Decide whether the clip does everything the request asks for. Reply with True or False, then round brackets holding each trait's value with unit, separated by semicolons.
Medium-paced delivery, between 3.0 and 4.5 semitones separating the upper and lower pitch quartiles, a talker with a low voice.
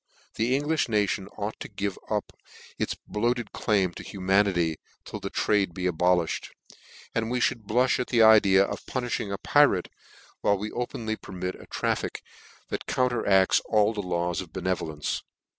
True (160 wpm; 3.7 semitones; 100 Hz)